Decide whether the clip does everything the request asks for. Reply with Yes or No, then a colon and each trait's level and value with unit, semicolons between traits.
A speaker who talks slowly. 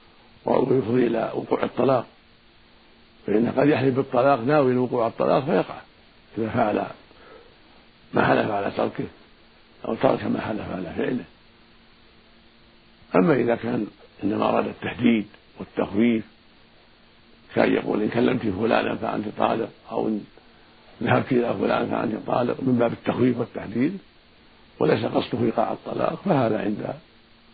No: average, 120 wpm